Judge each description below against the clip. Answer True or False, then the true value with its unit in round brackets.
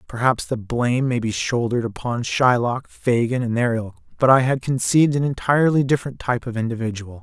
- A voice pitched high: False (120 Hz)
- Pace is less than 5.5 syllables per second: False (5.8 syllables/s)